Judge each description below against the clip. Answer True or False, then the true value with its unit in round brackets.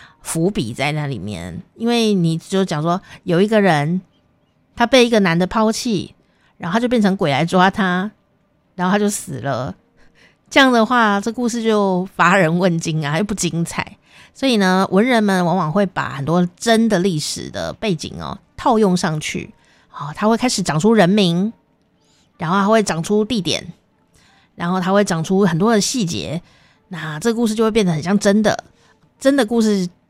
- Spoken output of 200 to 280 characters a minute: True (250 characters per minute)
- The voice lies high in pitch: True (195 Hz)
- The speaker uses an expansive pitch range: False (4.3 semitones)